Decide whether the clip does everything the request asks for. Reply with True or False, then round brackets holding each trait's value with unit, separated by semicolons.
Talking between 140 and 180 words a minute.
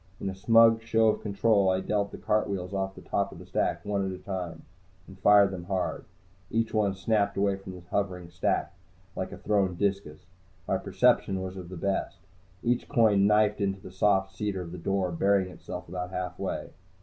False (195 wpm)